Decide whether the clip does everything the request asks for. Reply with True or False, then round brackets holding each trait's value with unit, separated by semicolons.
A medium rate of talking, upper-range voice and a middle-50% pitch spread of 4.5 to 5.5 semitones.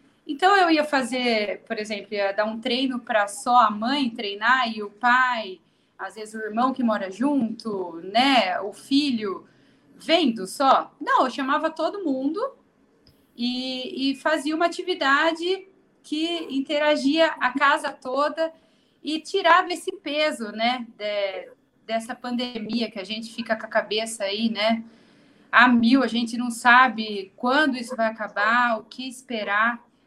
True (150 wpm; 250 Hz; 5.1 semitones)